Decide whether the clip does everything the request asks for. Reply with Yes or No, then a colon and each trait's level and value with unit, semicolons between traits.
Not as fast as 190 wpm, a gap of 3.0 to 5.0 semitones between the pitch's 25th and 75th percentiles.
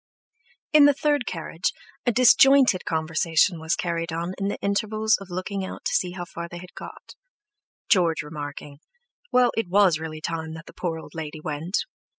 Yes: average, 175 wpm; average, 4.0 semitones